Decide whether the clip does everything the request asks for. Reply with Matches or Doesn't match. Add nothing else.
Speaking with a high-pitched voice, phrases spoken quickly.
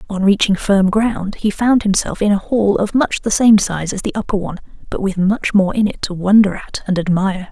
Matches